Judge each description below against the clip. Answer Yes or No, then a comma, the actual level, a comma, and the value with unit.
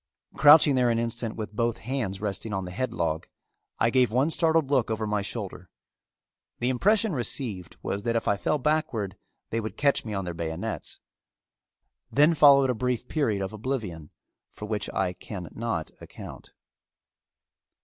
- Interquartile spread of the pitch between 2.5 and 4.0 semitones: No, average, 4.9 semitones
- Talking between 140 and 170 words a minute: Yes, average, 160 wpm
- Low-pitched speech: Yes, low, 115 Hz